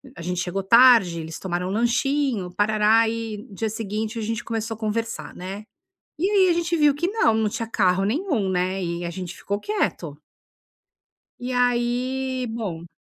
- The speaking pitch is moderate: No, high, 220 Hz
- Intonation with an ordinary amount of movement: Yes, average, 4.7 semitones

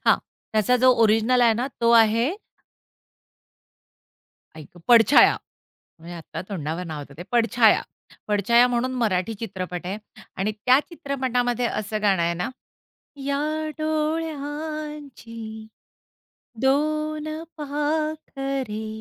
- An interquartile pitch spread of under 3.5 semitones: No, wide, 5.6 semitones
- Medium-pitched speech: No, high, 240 Hz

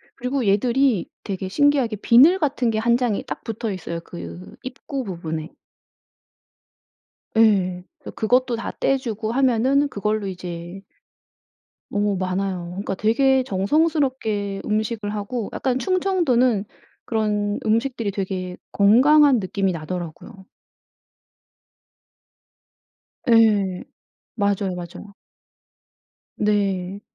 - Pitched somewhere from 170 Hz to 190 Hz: No, high, 210 Hz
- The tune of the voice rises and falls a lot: No, average, 4.7 semitones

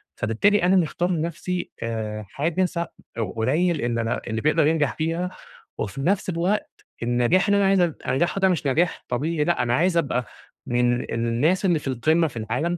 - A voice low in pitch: No, medium, 155 Hz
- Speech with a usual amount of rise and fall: No, wide, 6.4 semitones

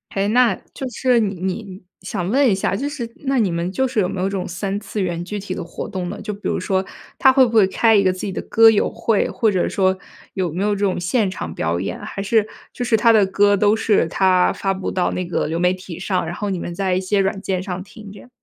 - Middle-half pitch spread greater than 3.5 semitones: No, average, 2.8 semitones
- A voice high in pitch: Yes, high, 195 Hz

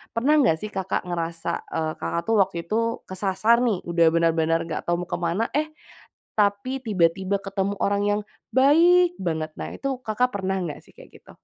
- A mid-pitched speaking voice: No, high, 195 Hz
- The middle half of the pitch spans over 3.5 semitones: Yes, average, 5.2 semitones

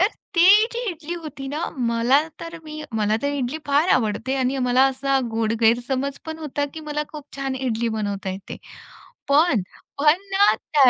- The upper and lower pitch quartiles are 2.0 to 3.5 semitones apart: No, average, 4.3 semitones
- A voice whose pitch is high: Yes, very high, 275 Hz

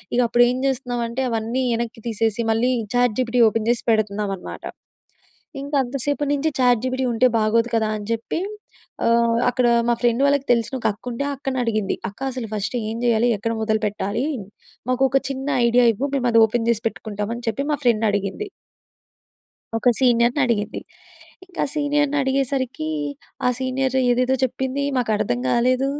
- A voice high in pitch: Yes, high, 240 Hz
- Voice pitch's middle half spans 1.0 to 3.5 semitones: Yes, average, 2.8 semitones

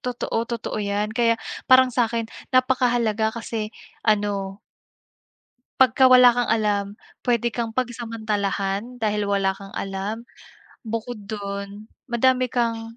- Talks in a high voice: Yes, high, 225 Hz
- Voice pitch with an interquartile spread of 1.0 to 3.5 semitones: Yes, average, 2.9 semitones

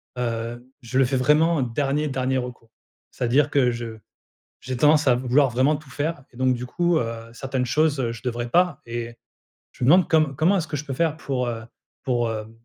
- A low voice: Yes, low, 130 Hz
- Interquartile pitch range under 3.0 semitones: No, average, 3.7 semitones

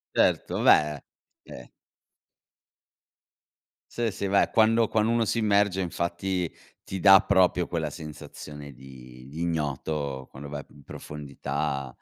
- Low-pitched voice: Yes, very low, 80 Hz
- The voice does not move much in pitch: No, average, 5.3 semitones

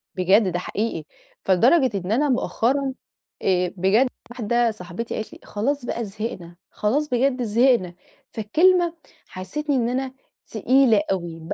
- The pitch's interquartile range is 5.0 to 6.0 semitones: Yes, wide, 5.5 semitones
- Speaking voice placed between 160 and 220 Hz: No, high, 230 Hz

